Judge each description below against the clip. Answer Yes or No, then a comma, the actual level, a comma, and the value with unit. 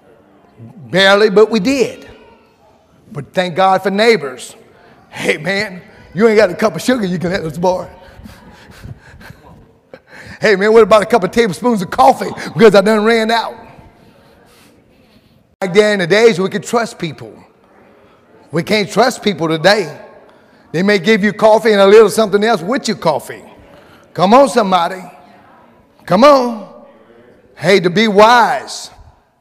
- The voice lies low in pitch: No, high, 205 Hz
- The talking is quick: No, average, 150 wpm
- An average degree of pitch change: Yes, average, 3.5 semitones